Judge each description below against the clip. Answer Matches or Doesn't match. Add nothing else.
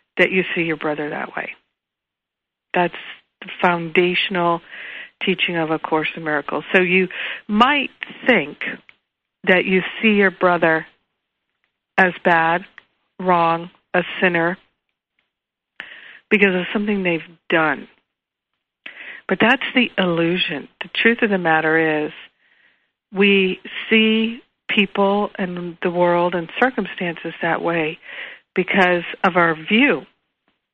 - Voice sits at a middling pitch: Matches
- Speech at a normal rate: Doesn't match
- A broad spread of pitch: Doesn't match